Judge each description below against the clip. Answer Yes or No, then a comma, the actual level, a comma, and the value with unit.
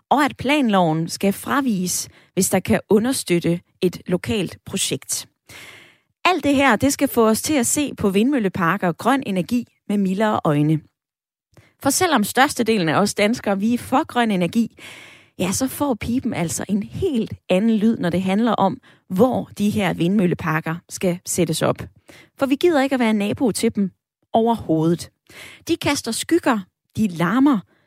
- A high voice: Yes, high, 215 Hz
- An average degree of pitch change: No, wide, 6.1 semitones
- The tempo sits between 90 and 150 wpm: No, average, 165 wpm